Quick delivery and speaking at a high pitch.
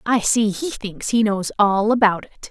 Yes: fast, 215 wpm; high, 215 Hz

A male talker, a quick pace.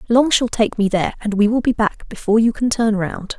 No: female; fast, 265 wpm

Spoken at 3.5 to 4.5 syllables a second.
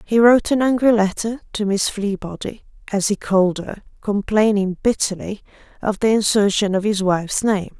No: 5.1 syllables/s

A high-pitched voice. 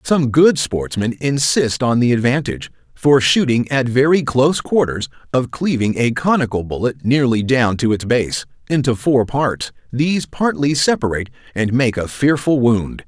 No: low, 130 Hz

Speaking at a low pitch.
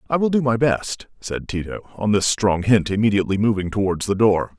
Yes: low, 105 Hz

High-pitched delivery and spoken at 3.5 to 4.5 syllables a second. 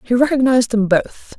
No: high, 240 Hz; 5.5 syllables/s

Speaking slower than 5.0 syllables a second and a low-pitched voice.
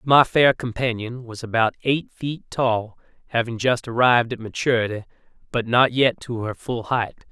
Yes: 4.7 syllables/s; low, 120 Hz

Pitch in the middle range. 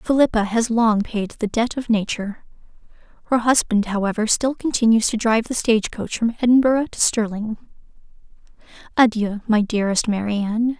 No: high, 225 Hz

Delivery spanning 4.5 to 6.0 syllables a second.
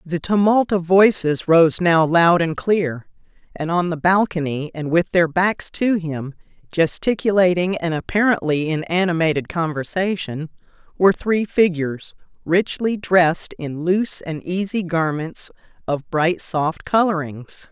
No: 4.2 syllables/s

